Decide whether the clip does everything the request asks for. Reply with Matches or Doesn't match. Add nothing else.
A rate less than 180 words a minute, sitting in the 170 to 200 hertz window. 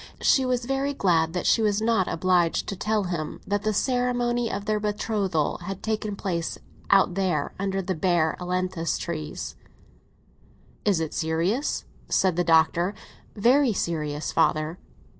Matches